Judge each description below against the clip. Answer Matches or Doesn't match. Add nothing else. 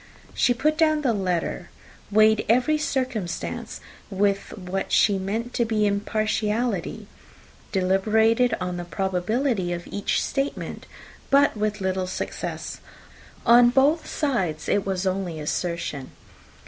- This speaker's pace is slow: Matches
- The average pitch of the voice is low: Doesn't match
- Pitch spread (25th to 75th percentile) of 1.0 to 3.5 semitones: Doesn't match